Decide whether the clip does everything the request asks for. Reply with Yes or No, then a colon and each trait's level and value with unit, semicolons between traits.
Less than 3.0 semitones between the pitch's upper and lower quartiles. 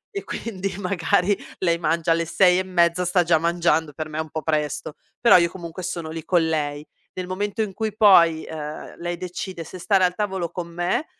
Yes: narrow, 2.5 semitones